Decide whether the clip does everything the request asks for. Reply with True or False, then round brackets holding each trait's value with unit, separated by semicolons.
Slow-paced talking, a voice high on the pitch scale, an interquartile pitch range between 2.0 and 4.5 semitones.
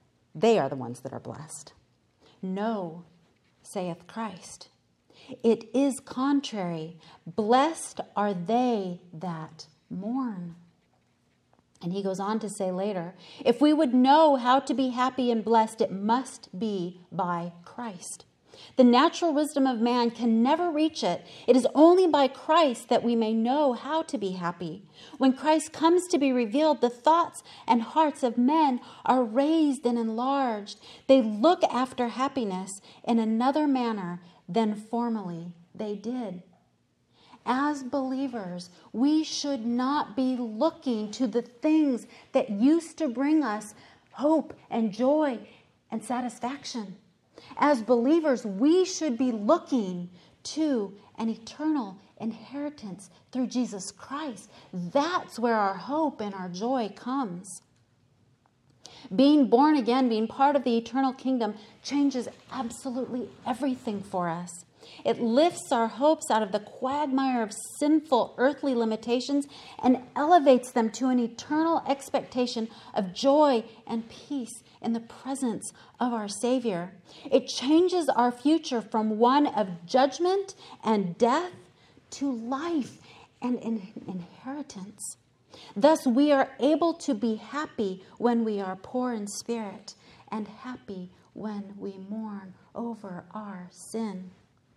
False (130 wpm; 240 Hz; 5.2 semitones)